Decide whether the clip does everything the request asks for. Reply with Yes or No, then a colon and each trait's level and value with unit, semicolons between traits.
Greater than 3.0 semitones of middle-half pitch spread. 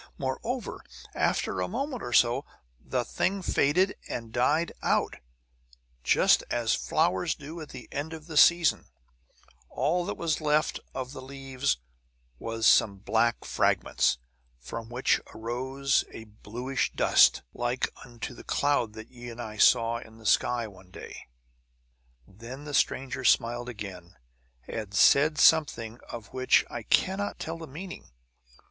Yes: average, 4.7 semitones